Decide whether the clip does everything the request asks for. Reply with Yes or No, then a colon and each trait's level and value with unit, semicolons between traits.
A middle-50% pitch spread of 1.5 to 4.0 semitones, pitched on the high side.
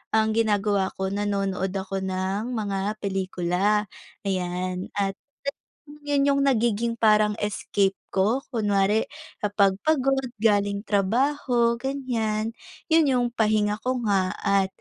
Yes: average, 3.1 semitones; high, 210 Hz